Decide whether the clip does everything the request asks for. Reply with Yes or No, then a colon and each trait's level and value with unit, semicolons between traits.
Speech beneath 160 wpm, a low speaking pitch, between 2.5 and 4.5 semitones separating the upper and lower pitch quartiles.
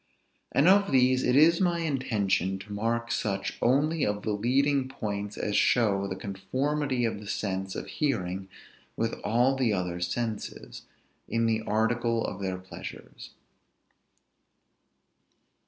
No: slow, 135 wpm; low, 115 Hz; average, 4.9 semitones